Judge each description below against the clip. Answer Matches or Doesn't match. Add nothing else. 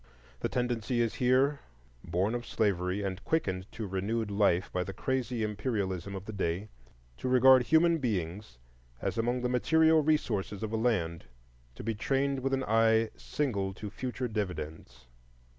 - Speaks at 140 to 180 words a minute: Matches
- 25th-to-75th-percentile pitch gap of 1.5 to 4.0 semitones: Doesn't match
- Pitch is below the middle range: Matches